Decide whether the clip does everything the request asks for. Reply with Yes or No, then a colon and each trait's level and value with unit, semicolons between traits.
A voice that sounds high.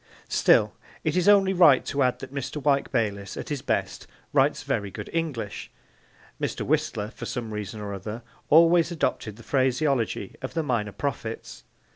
No: low, 130 Hz